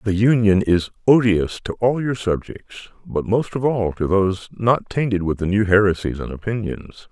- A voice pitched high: No, low, 105 Hz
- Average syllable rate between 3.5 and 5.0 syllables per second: Yes, 4.7 syllables/s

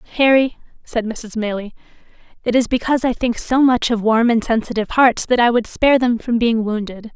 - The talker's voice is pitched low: No, high, 235 Hz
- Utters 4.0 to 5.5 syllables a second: No, 5.7 syllables/s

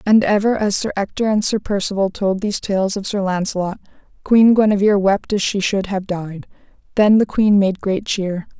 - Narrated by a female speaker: Yes, female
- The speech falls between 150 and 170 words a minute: No, average, 195 wpm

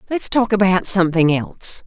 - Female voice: No, male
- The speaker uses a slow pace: No, average, 160 wpm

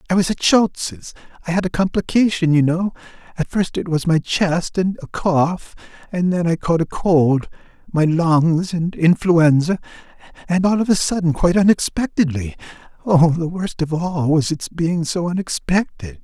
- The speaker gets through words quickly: No, average, 165 wpm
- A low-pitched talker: No, medium, 170 Hz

